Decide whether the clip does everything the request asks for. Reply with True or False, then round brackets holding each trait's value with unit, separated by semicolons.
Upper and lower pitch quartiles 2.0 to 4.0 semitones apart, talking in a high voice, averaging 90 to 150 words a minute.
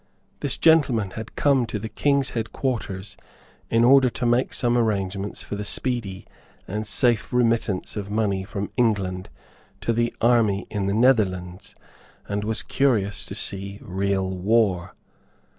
False (3.5 semitones; 110 Hz; 140 wpm)